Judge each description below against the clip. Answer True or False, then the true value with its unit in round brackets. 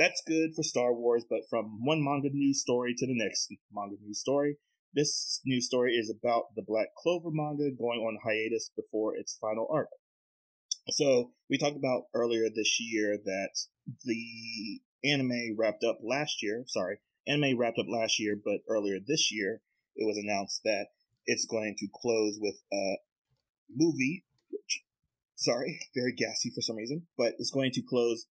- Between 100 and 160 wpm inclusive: False (170 wpm)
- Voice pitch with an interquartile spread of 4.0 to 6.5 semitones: True (4.4 semitones)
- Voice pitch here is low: True (120 Hz)